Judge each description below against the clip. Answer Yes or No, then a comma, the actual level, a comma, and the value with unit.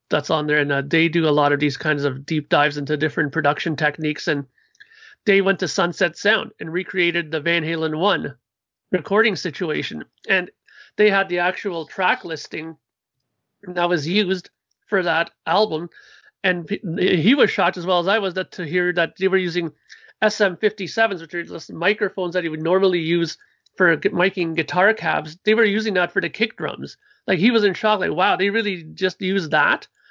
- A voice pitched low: No, medium, 180 Hz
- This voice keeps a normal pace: Yes, average, 195 wpm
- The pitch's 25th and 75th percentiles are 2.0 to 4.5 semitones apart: Yes, average, 3.9 semitones